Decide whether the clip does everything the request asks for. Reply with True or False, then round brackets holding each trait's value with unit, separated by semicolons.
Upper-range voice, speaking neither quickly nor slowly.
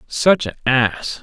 False (140 Hz; 145 wpm)